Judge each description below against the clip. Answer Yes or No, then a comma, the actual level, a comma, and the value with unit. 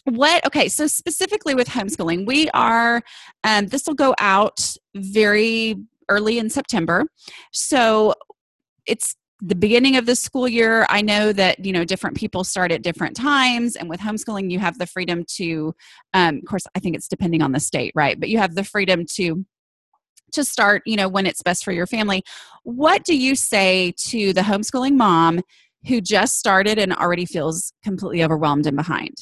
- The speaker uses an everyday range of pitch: Yes, average, 5.0 semitones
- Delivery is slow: No, average, 185 wpm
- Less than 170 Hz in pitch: No, high, 205 Hz